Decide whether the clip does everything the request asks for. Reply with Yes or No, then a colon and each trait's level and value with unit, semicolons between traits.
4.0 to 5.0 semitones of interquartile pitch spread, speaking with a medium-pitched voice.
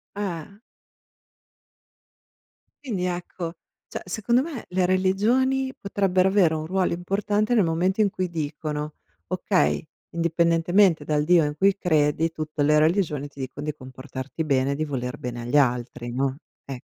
Yes: average, 4.6 semitones; medium, 165 Hz